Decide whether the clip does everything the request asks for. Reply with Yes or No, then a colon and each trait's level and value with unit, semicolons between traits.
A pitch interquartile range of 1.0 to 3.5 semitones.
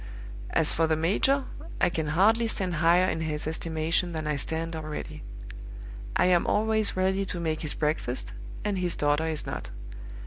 Yes: average, 3.0 semitones